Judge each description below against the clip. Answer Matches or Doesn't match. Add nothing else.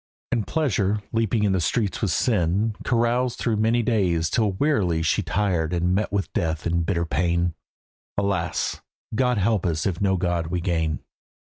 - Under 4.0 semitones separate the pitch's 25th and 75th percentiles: Doesn't match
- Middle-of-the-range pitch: Doesn't match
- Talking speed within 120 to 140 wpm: Doesn't match